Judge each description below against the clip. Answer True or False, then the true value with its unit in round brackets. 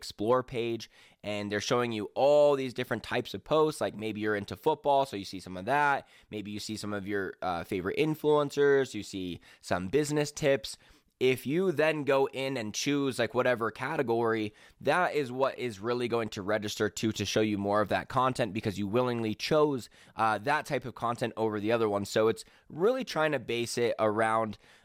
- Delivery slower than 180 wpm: False (205 wpm)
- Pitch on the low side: True (120 Hz)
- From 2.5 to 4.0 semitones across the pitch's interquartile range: False (4.5 semitones)